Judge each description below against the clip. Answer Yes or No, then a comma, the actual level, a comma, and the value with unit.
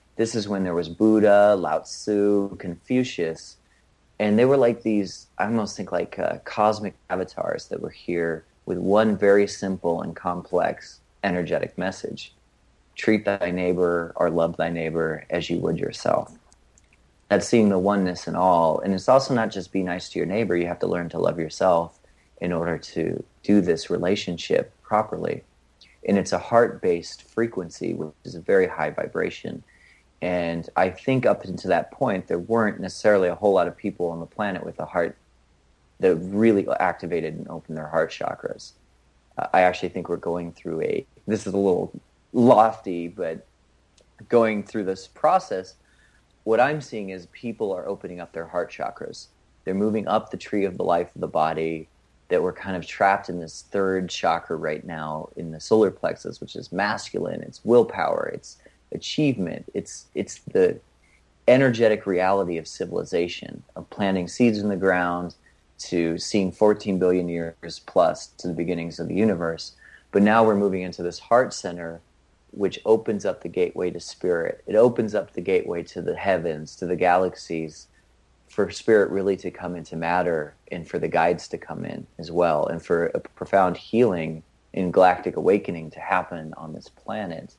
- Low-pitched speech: Yes, very low, 90 Hz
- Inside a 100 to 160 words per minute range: No, average, 175 wpm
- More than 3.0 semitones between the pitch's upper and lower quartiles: Yes, average, 3.9 semitones